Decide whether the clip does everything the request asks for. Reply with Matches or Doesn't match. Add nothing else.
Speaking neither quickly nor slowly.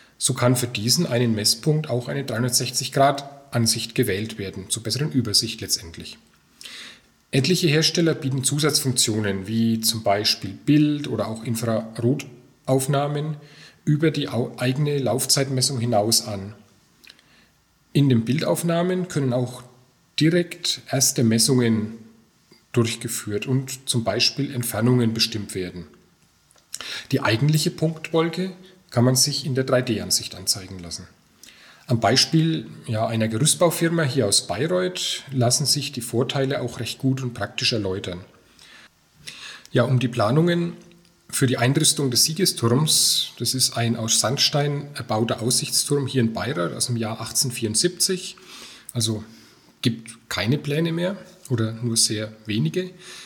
Doesn't match